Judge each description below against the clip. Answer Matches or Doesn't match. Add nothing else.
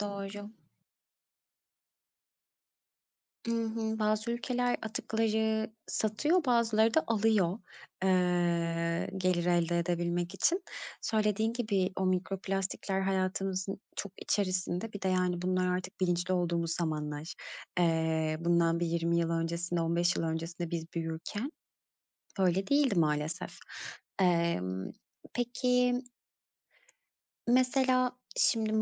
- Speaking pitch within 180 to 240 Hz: Matches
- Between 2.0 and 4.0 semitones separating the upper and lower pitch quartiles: Doesn't match